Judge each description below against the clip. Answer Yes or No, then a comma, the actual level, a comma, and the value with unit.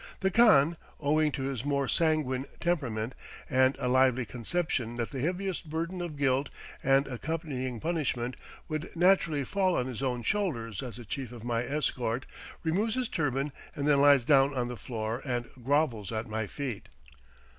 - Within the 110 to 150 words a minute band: No, average, 165 wpm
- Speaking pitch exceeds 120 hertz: Yes, low, 135 Hz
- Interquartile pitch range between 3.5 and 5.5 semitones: Yes, average, 4.4 semitones